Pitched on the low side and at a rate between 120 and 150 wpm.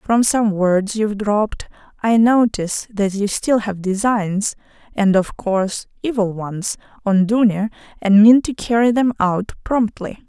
No: high, 210 Hz; average, 140 wpm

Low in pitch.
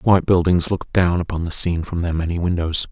Yes: very low, 85 Hz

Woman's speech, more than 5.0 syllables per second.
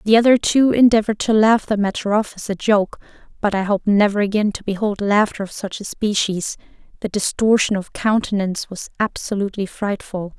Yes: female; 5.5 syllables/s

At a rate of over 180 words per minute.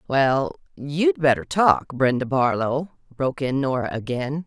No: slow, 135 wpm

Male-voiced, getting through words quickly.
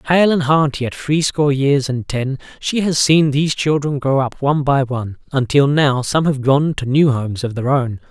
Yes: male; fast, 220 wpm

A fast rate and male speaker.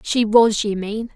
No: fast, 210 wpm; female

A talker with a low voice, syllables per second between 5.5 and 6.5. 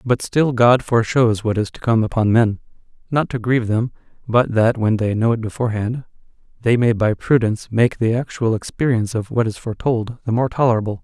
Yes: low, 115 Hz; 5.8 syllables/s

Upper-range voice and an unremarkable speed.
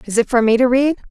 No: high, 245 Hz; fast, 325 wpm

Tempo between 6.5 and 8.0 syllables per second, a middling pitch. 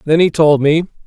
No: 5.4 syllables/s; medium, 155 Hz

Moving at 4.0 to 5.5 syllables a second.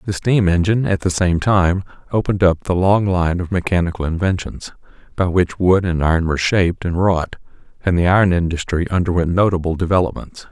No: 5.8 syllables/s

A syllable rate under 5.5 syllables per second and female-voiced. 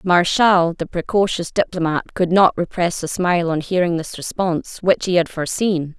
Yes: 5.0 syllables/s; female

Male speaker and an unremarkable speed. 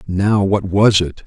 Yes: male; average, 190 wpm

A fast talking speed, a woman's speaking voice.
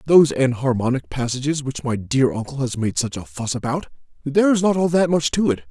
No: fast, 210 wpm; male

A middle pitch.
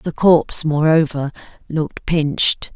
Yes: medium, 155 Hz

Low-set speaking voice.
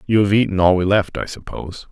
Yes: low, 100 Hz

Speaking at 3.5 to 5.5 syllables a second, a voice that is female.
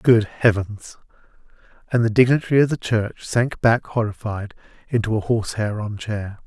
No: 4.9 syllables/s; male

